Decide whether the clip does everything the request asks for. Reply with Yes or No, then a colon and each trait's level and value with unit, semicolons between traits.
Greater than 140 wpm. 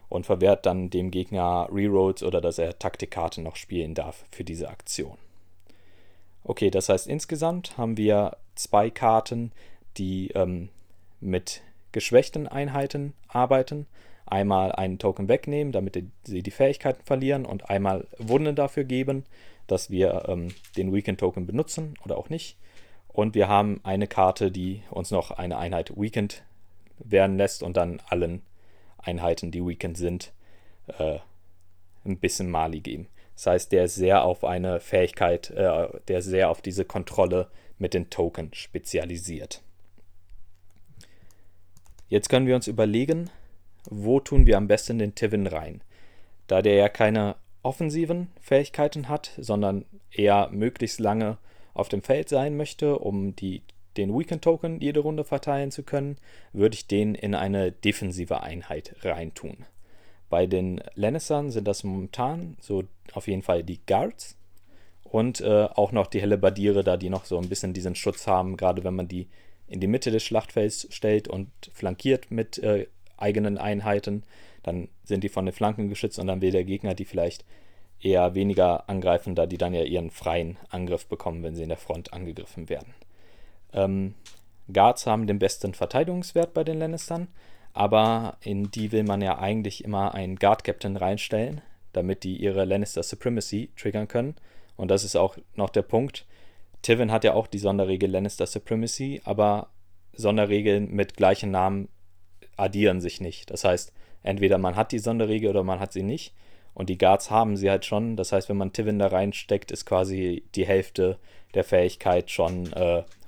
Yes: average, 160 wpm